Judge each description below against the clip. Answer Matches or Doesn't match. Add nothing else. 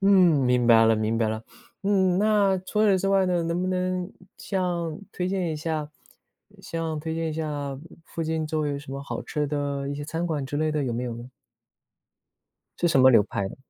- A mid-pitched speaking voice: Matches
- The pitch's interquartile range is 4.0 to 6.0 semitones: Matches